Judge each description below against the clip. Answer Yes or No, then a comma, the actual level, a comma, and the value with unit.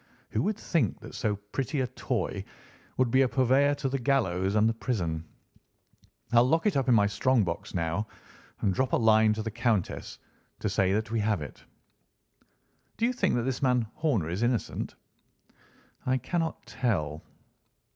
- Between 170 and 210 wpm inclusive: Yes, average, 175 wpm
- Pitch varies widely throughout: No, average, 4.4 semitones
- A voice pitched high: No, low, 115 Hz